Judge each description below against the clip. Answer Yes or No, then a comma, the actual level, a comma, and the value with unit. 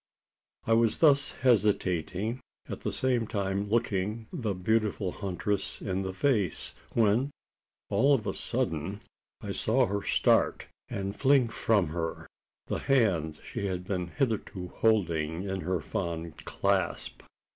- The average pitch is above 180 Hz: No, low, 100 Hz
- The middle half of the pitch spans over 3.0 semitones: Yes, average, 3.9 semitones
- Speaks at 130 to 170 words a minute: Yes, slow, 135 wpm